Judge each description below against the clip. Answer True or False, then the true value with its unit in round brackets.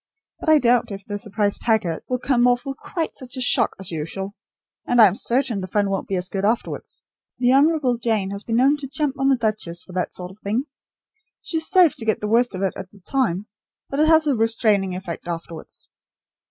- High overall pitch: True (225 Hz)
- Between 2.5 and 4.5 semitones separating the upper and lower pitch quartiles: False (5.2 semitones)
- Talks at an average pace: False (230 wpm)